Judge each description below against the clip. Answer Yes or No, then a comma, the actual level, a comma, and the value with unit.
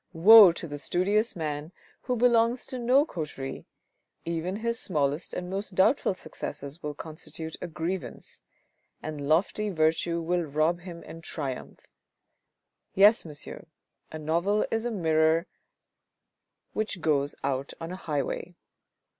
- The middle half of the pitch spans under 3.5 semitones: No, average, 4.5 semitones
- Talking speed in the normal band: No, slow, 130 wpm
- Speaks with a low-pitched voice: No, medium, 170 Hz